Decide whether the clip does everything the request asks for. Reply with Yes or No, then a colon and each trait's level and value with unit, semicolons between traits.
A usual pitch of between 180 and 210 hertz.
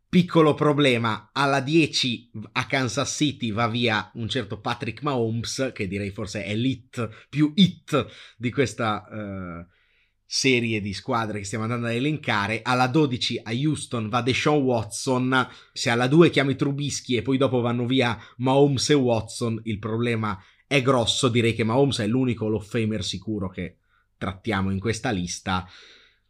No: low, 120 Hz